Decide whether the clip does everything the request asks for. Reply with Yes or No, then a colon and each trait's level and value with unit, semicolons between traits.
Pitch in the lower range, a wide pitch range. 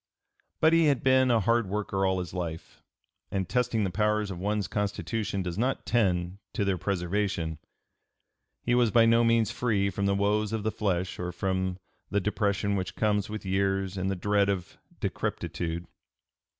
No: low, 100 Hz; average, 2.7 semitones